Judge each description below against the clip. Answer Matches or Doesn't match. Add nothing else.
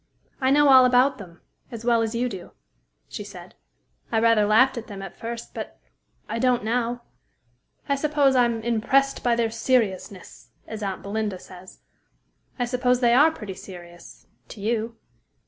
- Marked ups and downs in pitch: Doesn't match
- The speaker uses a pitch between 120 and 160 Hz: Doesn't match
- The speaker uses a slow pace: Doesn't match